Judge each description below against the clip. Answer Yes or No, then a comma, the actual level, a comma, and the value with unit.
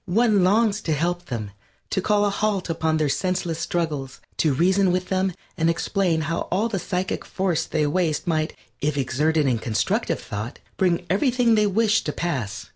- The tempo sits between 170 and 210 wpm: Yes, average, 180 wpm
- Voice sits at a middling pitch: Yes, medium, 175 Hz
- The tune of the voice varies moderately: Yes, average, 4.2 semitones